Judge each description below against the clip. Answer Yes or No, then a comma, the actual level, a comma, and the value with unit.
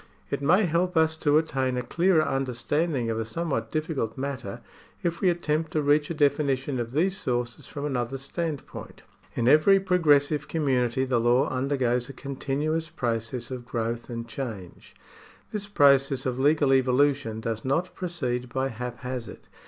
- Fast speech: No, average, 160 wpm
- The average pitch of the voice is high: No, low, 135 Hz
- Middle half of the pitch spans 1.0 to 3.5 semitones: No, average, 4.1 semitones